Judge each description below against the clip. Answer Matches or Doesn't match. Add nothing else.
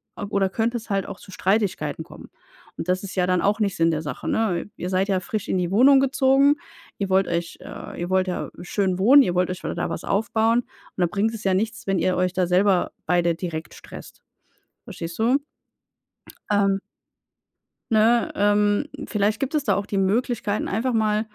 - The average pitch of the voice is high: Matches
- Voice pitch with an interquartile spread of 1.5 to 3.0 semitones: Doesn't match